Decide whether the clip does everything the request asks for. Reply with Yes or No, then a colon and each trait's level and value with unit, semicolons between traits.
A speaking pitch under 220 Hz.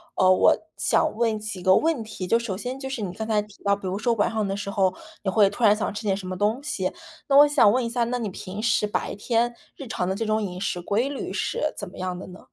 Yes: high, 210 Hz